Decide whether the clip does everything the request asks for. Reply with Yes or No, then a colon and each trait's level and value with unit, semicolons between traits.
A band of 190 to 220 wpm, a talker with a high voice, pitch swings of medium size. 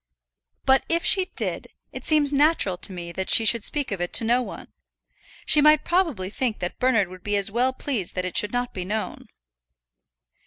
No: average, 200 wpm; high, 230 Hz; wide, 7.0 semitones